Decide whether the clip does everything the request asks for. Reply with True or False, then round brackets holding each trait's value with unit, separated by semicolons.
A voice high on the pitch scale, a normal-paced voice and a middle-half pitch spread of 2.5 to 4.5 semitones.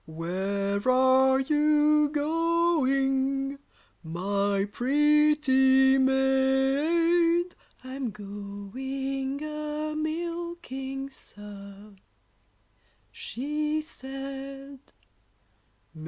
False (270 Hz; 55 wpm; 2.8 semitones)